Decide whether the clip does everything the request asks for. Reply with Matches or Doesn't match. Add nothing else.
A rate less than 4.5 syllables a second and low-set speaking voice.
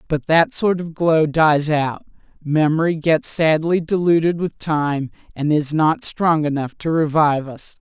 Doesn't match